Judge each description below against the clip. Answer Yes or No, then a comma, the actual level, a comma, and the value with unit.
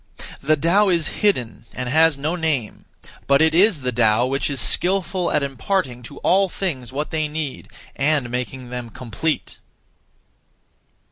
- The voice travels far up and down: No, average, 4.9 semitones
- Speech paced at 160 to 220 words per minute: No, average, 150 wpm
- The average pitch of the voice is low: No, medium, 145 Hz